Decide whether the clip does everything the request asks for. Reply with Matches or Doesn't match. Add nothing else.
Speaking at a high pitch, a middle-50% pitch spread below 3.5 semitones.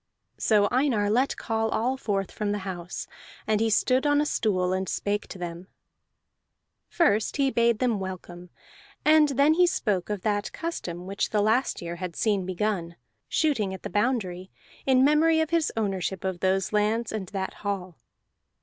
Doesn't match